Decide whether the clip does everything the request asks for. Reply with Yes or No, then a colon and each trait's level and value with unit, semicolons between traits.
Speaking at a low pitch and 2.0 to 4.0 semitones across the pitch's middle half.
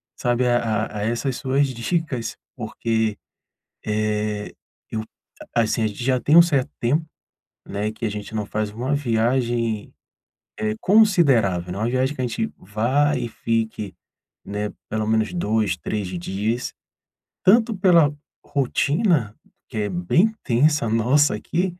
No: low, 115 Hz; average, 4.7 semitones